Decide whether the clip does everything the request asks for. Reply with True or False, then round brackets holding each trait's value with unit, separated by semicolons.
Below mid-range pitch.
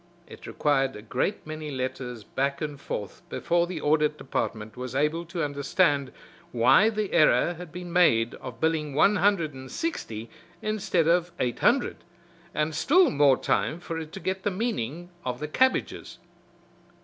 False (155 Hz)